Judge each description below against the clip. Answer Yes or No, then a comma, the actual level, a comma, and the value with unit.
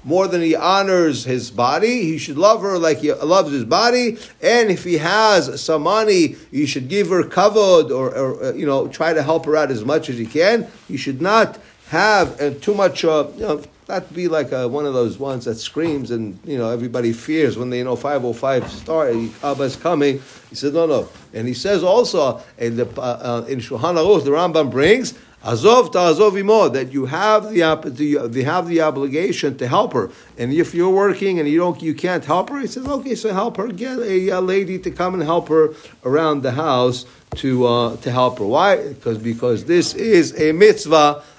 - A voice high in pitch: No, medium, 155 Hz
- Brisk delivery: Yes, fast, 215 wpm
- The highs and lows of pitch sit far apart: Yes, wide, 6.3 semitones